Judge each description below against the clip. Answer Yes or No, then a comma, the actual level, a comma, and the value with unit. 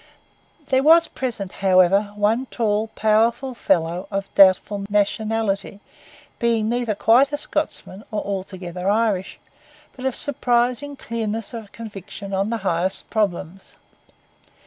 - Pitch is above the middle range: Yes, high, 215 Hz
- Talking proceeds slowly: Yes, slow, 115 wpm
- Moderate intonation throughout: Yes, average, 3.2 semitones